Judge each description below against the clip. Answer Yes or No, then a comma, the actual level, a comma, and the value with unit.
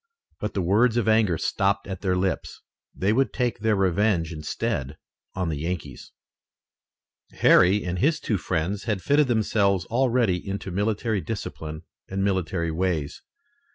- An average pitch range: Yes, average, 3.8 semitones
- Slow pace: No, average, 145 wpm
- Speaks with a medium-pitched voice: No, very low, 95 Hz